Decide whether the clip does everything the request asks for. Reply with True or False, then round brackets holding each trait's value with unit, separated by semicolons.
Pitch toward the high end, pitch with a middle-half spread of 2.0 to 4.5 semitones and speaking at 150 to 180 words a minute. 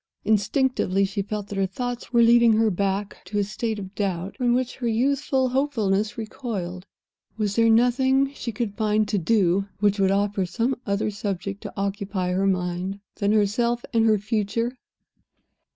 True (210 Hz; 3.2 semitones; 170 wpm)